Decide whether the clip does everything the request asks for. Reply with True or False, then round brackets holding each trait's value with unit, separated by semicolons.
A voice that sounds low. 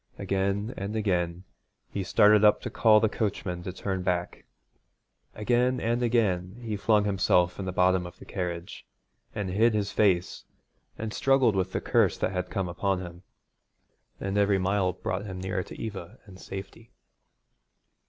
True (100 Hz)